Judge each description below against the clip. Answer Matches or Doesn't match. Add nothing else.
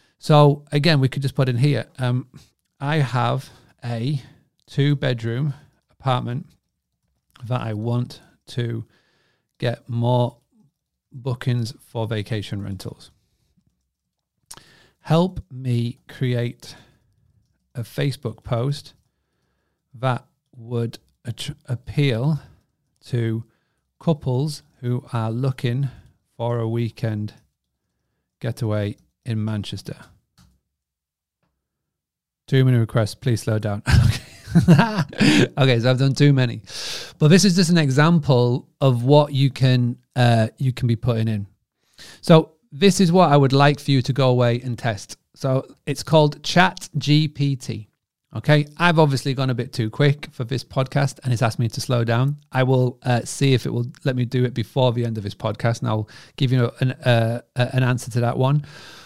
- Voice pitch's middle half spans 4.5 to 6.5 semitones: Doesn't match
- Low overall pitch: Matches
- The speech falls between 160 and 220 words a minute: Doesn't match